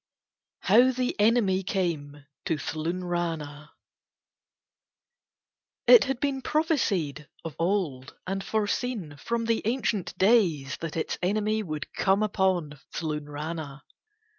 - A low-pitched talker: No, medium, 185 Hz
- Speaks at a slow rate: Yes, slow, 105 wpm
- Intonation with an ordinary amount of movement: No, wide, 6.2 semitones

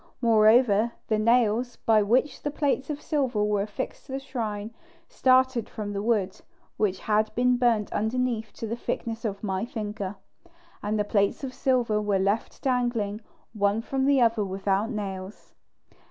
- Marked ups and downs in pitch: No, average, 3.1 semitones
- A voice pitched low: No, high, 220 Hz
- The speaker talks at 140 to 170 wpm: Yes, average, 160 wpm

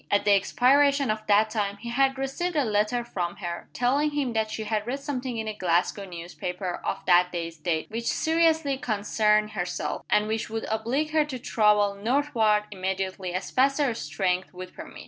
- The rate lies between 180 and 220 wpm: Yes, average, 190 wpm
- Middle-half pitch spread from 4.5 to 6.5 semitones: Yes, wide, 5.6 semitones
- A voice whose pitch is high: Yes, high, 215 Hz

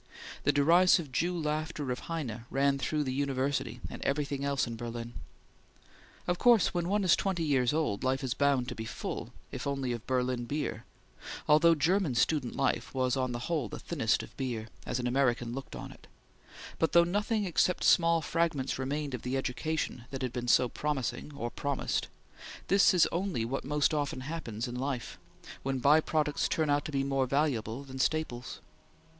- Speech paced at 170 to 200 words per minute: Yes, average, 185 wpm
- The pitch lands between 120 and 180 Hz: Yes, medium, 140 Hz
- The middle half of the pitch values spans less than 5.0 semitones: Yes, average, 3.9 semitones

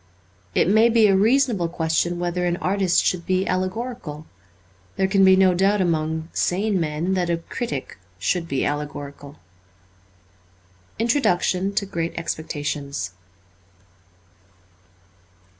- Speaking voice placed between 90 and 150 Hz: No, medium, 180 Hz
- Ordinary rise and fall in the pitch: Yes, average, 3.4 semitones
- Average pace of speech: No, slow, 115 wpm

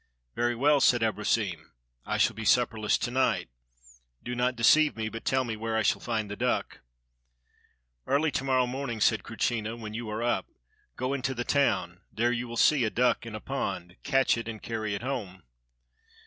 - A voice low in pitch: Yes, low, 115 Hz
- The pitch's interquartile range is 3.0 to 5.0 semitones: No, narrow, 2.6 semitones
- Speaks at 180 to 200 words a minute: Yes, average, 190 wpm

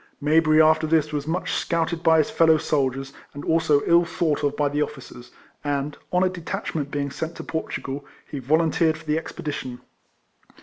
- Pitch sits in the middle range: Yes, medium, 155 Hz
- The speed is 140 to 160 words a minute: No, average, 180 wpm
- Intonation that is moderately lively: No, narrow, 2.1 semitones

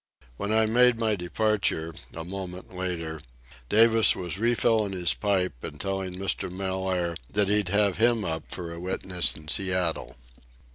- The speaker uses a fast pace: No, average, 150 wpm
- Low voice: Yes, very low, 95 Hz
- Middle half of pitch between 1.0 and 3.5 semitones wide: Yes, average, 3.1 semitones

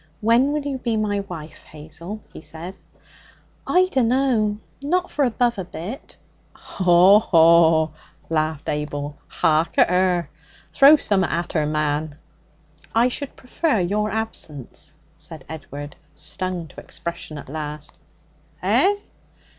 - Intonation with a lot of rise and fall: Yes, wide, 6.6 semitones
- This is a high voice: No, medium, 180 Hz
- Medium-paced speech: No, slow, 125 wpm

